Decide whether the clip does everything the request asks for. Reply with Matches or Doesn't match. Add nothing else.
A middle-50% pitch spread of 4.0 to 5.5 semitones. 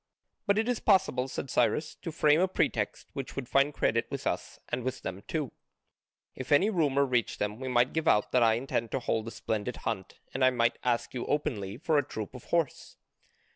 Matches